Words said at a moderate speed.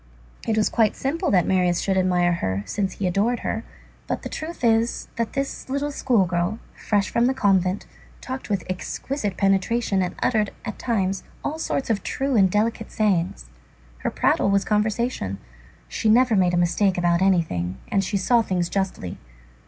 Yes: average, 175 wpm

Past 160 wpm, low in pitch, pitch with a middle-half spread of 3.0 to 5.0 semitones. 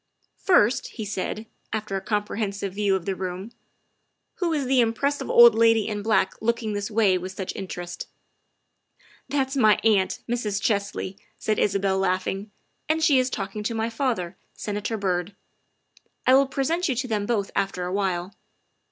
No: average, 185 wpm; high, 210 Hz; average, 3.5 semitones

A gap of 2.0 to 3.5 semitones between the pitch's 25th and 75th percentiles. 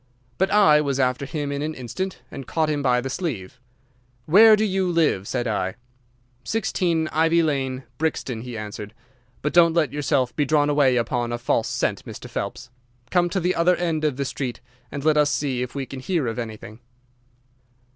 No: average, 4.7 semitones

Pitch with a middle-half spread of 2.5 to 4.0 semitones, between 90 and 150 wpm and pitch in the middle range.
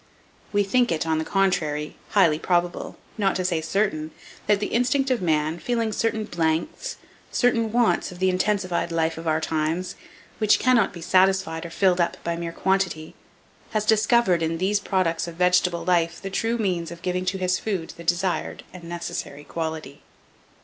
No: average, 3.6 semitones; average, 175 wpm; medium, 180 Hz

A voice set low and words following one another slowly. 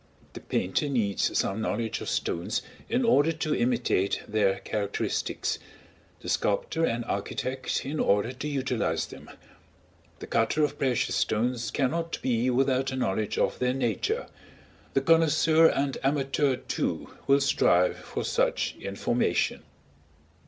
Yes: low, 130 Hz; slow, 130 wpm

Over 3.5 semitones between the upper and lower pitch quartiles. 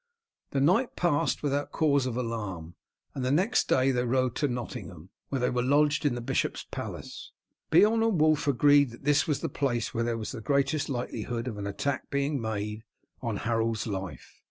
Yes: average, 4.0 semitones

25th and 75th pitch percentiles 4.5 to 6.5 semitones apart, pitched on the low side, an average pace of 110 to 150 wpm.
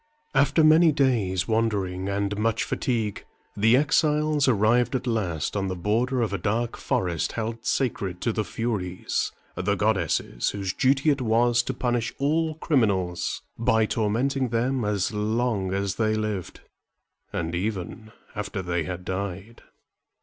No: average, 4.0 semitones; low, 110 Hz; average, 140 wpm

